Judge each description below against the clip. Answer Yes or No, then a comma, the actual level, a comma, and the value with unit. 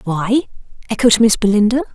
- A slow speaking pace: Yes, slow, 125 wpm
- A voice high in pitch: Yes, high, 220 Hz